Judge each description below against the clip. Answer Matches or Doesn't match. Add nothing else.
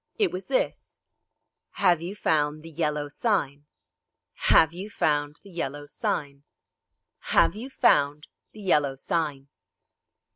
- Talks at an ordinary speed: Doesn't match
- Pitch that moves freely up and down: Doesn't match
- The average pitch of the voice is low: Doesn't match